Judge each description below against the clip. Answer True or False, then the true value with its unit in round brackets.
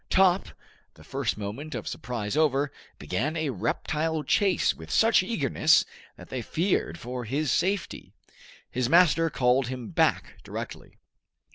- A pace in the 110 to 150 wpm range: True (135 wpm)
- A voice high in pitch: False (140 Hz)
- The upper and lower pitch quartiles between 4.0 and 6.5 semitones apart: True (5.2 semitones)